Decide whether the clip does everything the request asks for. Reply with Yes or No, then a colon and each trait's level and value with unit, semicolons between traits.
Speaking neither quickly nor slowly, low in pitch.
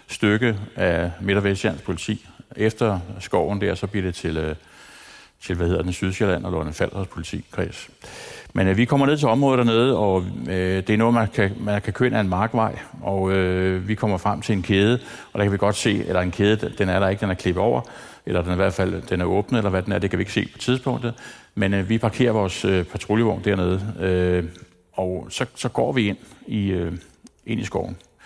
No: fast, 230 wpm; low, 100 Hz